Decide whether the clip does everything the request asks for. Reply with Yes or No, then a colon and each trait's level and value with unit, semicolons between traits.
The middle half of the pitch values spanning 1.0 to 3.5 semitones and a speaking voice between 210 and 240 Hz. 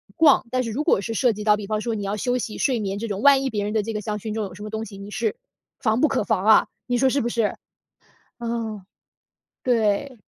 Yes: average, 2.9 semitones; high, 220 Hz